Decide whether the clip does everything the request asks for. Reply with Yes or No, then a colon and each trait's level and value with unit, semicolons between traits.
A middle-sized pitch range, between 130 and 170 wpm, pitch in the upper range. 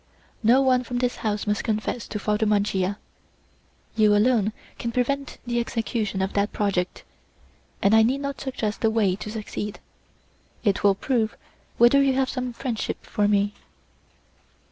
Yes: average, 3.2 semitones; average, 155 wpm; high, 220 Hz